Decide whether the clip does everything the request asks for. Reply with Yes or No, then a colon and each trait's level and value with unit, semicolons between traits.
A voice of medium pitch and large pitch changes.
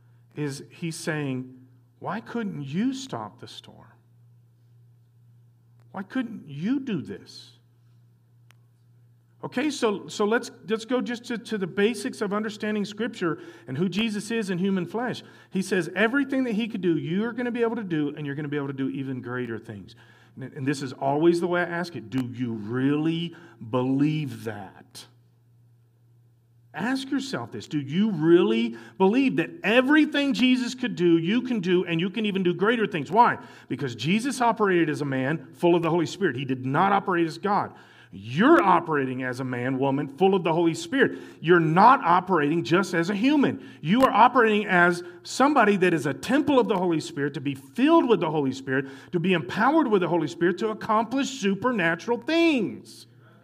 Yes: medium, 170 Hz; wide, 9.0 semitones